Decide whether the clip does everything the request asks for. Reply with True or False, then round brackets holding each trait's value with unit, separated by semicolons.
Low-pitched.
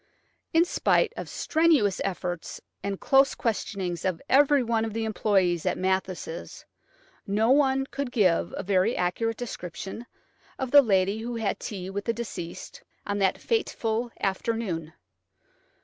False (215 Hz)